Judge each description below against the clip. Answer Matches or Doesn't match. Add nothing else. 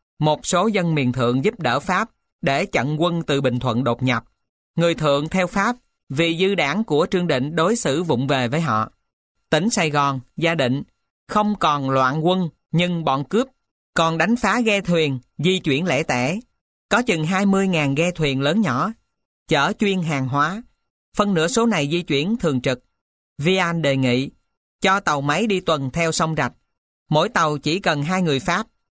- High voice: Doesn't match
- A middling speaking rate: Matches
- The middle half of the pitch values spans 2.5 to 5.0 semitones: Doesn't match